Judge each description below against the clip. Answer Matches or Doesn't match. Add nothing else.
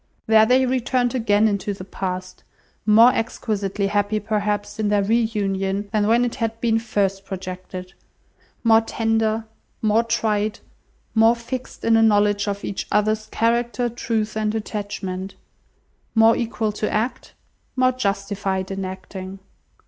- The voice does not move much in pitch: Matches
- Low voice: Doesn't match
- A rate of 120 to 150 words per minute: Matches